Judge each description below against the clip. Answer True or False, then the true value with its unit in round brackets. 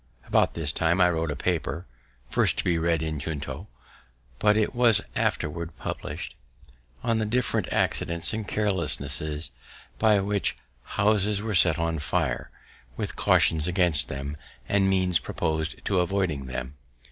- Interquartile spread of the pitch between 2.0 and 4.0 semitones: False (4.6 semitones)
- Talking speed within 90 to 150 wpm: True (145 wpm)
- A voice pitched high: False (85 Hz)